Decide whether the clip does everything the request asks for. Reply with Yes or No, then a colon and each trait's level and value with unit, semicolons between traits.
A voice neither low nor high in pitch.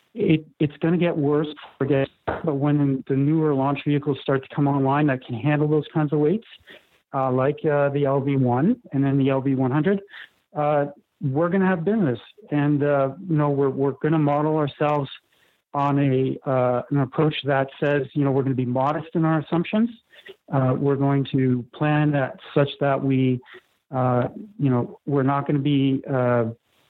Yes: medium, 145 Hz